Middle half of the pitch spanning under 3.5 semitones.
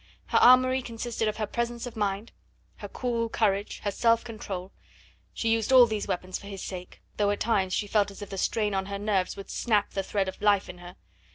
Yes: average, 2.9 semitones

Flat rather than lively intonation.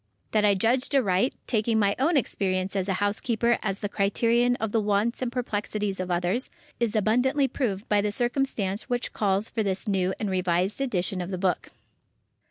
No: average, 3.7 semitones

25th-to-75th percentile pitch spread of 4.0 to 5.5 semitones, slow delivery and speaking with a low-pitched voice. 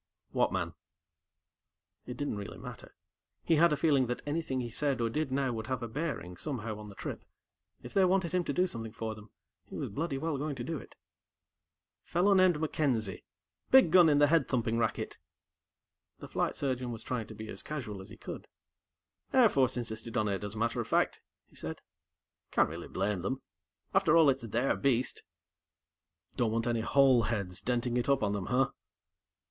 No: average, 5.0 semitones; average, 195 wpm; low, 125 Hz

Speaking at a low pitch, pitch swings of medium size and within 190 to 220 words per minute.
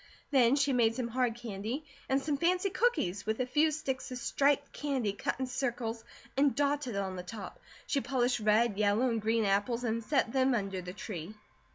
No: high, 240 Hz; average, 4.2 semitones; average, 195 wpm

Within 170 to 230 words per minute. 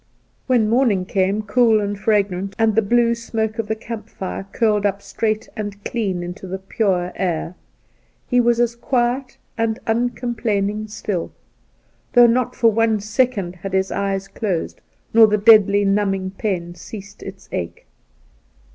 No: average, 150 wpm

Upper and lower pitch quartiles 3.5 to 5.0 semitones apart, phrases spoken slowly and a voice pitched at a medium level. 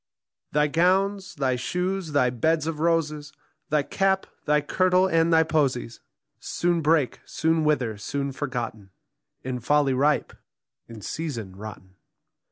Yes: average, 4.4 semitones; slow, 130 wpm; medium, 150 Hz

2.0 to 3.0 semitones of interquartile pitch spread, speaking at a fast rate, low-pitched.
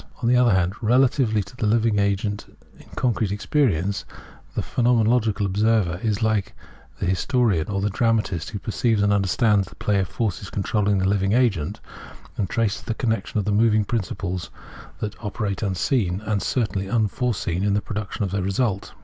No: average, 2.7 semitones; average, 175 wpm; low, 105 Hz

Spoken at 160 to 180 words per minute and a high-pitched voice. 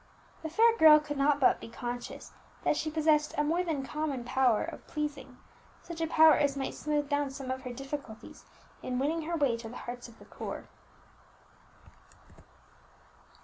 Yes: average, 175 wpm; very high, 290 Hz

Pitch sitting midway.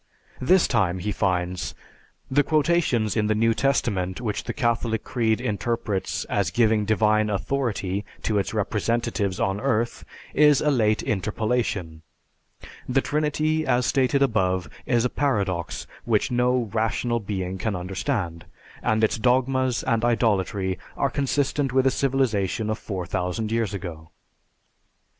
No: low, 110 Hz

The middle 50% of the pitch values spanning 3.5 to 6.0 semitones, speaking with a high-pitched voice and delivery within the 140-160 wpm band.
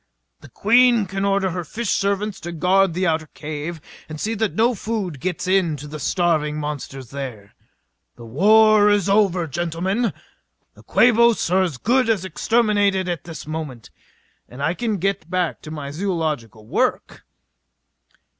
No: average, 5.0 semitones; medium, 180 Hz; average, 155 wpm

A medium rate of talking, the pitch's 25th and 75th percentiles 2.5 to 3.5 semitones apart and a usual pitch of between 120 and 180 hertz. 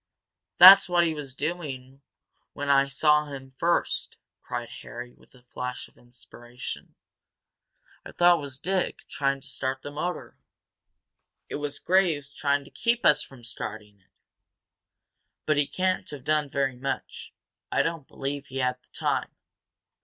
Yes: average, 155 wpm; average, 2.8 semitones; medium, 140 Hz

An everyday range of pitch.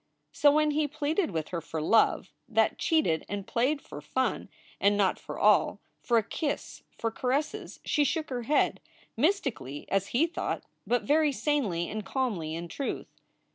No: wide, 7.3 semitones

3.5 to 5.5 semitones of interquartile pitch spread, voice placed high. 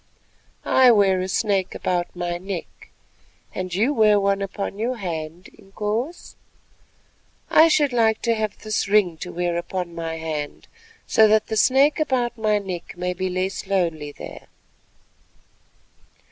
Yes: average, 3.8 semitones; high, 195 Hz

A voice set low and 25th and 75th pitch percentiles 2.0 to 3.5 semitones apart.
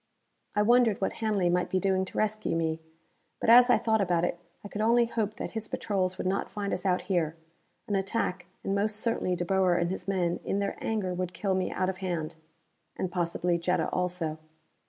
No: high, 190 Hz; average, 2.8 semitones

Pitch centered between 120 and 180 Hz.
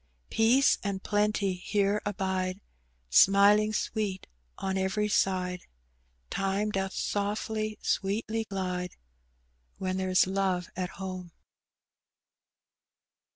No: high, 195 Hz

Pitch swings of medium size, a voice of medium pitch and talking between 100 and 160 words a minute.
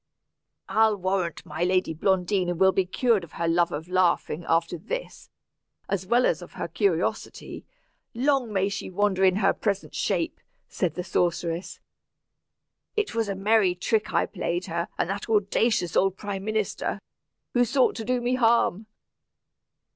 No: average, 3.9 semitones; high, 195 Hz; average, 155 wpm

